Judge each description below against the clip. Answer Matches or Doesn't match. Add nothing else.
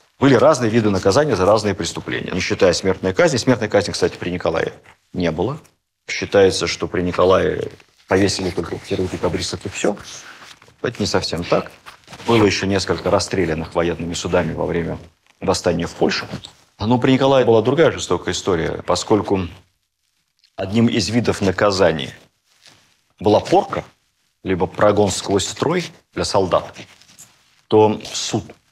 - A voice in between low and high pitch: Doesn't match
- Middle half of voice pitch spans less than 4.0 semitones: Matches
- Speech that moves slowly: Doesn't match